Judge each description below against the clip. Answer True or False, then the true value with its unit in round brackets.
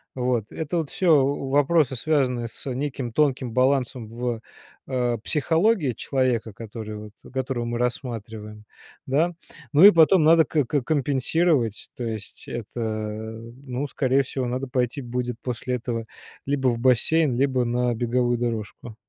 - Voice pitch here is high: False (125 Hz)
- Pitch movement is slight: False (3.1 semitones)